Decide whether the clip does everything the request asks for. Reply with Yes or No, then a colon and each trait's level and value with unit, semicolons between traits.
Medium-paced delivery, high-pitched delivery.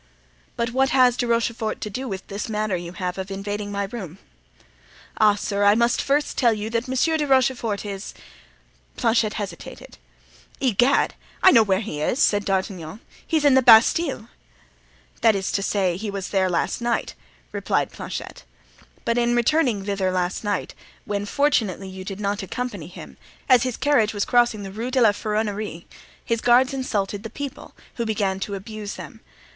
Yes: average, 170 wpm; high, 215 Hz